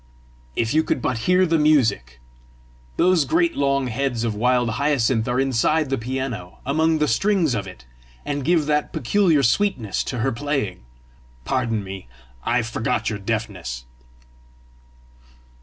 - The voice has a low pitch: Yes, low, 130 Hz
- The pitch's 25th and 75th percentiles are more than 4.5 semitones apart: Yes, average, 5.1 semitones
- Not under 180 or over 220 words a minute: No, average, 140 wpm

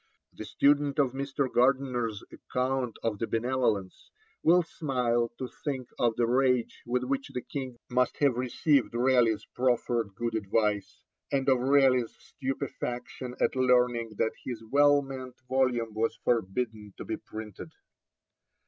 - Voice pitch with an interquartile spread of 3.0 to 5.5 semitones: No, narrow, 2.5 semitones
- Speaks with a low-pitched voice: Yes, low, 125 Hz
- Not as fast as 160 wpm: Yes, average, 140 wpm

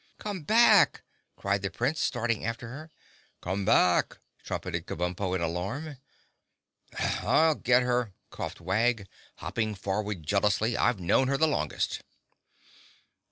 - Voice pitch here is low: Yes, low, 110 Hz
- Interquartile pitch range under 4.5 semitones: No, wide, 5.6 semitones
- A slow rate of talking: Yes, slow, 120 wpm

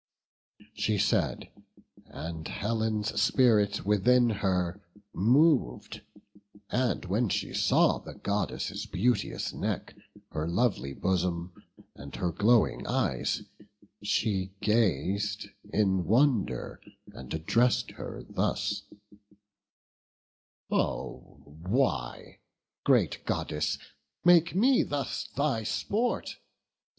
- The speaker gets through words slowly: Yes, slow, 90 wpm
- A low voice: Yes, low, 105 Hz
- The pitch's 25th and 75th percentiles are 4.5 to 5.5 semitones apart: Yes, average, 5.2 semitones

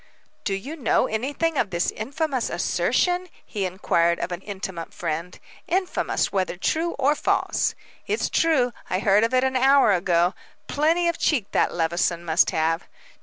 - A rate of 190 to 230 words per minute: No, average, 160 wpm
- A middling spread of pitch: No, wide, 8.5 semitones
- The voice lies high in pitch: Yes, high, 215 Hz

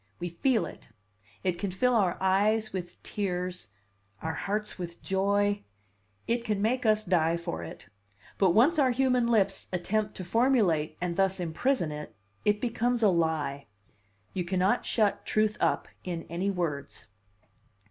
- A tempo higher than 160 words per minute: No, average, 150 wpm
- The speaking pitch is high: Yes, high, 195 Hz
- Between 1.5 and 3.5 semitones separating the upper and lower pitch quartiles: No, average, 4.0 semitones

